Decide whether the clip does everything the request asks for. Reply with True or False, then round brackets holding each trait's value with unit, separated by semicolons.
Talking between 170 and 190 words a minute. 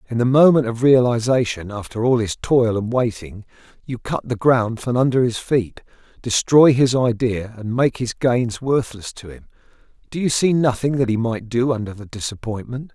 True (185 wpm)